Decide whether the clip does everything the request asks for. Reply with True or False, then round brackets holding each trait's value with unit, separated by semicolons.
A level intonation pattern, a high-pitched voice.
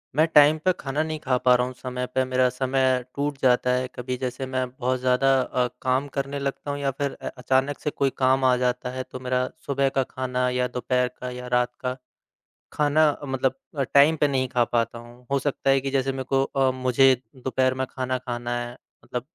False (1.3 semitones; 130 Hz)